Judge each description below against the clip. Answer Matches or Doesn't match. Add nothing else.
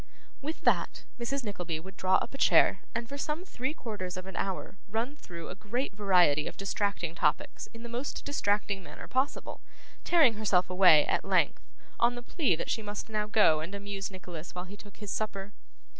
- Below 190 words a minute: Doesn't match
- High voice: Matches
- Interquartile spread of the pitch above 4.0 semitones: Matches